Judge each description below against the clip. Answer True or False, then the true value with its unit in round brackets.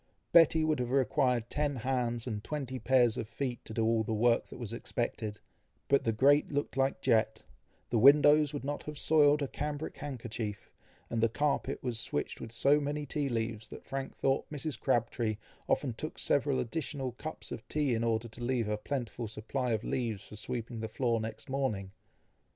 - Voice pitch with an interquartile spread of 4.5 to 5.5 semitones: False (4.1 semitones)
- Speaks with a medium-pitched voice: False (125 Hz)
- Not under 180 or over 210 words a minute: True (190 wpm)